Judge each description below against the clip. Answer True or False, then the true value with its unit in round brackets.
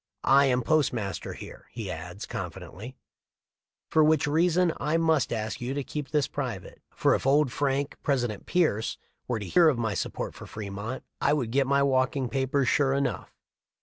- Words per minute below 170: False (175 wpm)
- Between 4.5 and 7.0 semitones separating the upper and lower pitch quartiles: False (4.1 semitones)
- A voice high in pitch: False (135 Hz)